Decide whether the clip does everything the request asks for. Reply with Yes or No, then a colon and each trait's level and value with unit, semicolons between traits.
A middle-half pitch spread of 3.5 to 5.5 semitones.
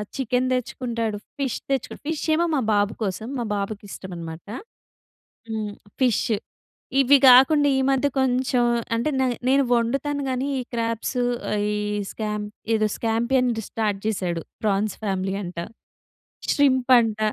Yes: average, 3.8 semitones